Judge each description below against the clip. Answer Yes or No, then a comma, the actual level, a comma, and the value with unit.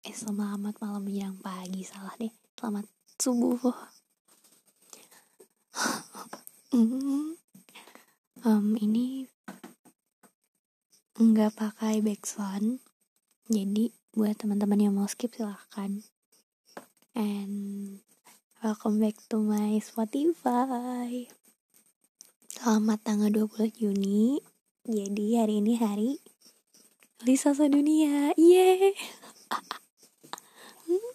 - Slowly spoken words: Yes, slow, 75 wpm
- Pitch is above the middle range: Yes, high, 220 Hz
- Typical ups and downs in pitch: Yes, average, 3.0 semitones